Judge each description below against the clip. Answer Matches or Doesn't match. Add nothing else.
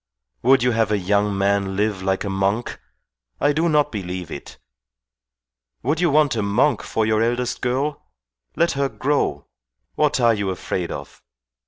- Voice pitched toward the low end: Matches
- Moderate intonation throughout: Doesn't match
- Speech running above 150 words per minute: Matches